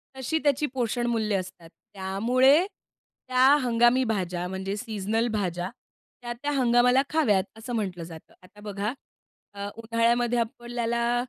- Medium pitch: No, high, 230 Hz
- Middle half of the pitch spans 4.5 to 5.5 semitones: No, average, 3.7 semitones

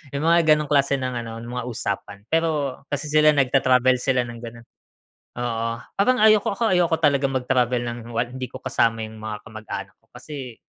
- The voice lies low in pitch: Yes, low, 130 Hz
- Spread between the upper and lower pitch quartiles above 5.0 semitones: No, average, 4.2 semitones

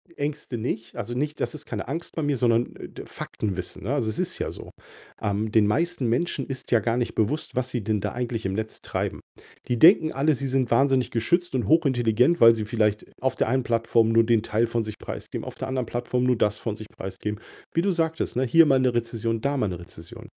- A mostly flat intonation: No, average, 3.7 semitones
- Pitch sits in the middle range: No, low, 120 Hz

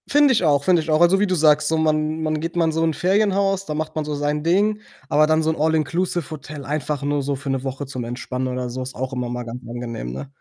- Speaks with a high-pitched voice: No, medium, 155 Hz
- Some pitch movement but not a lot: Yes, average, 3.5 semitones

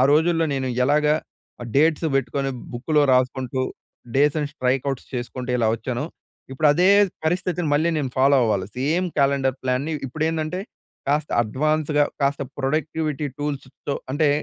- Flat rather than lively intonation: No, average, 3.0 semitones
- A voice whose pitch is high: No, medium, 145 Hz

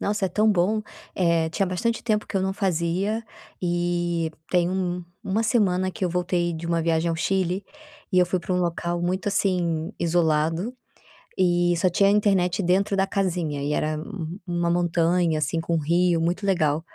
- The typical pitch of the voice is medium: Yes, medium, 175 Hz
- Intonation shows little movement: Yes, narrow, 2.3 semitones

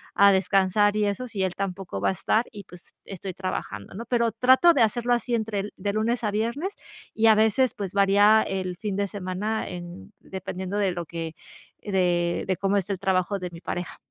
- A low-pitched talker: No, high, 200 Hz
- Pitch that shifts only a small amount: No, average, 3.0 semitones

